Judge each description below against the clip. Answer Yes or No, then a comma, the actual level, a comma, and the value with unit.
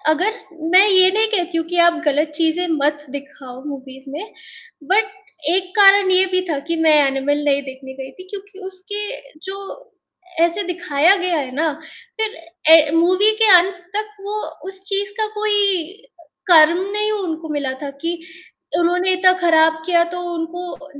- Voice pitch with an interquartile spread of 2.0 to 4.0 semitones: No, average, 4.4 semitones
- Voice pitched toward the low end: No, very high, 345 Hz